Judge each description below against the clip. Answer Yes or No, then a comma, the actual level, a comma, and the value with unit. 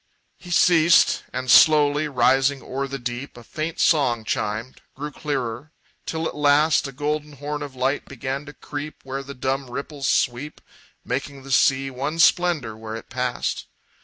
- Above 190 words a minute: No, average, 160 wpm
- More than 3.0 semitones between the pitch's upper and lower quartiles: No, average, 2.7 semitones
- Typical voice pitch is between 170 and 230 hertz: No, medium, 140 Hz